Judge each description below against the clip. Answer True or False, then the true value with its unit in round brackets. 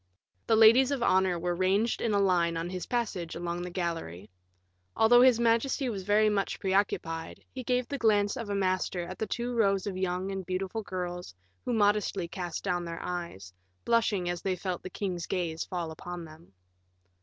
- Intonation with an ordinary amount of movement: True (3.7 semitones)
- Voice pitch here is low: False (190 Hz)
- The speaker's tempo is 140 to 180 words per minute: False (190 wpm)